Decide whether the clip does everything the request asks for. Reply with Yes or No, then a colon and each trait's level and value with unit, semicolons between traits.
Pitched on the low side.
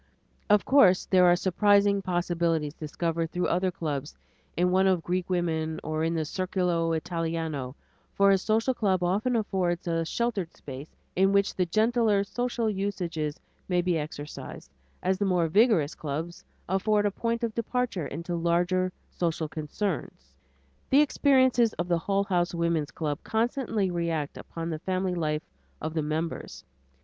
No: medium, 180 Hz